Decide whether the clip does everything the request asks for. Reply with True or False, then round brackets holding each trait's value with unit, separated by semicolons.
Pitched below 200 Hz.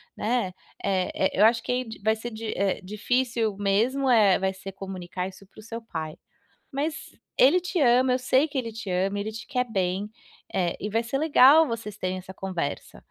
False (220 Hz)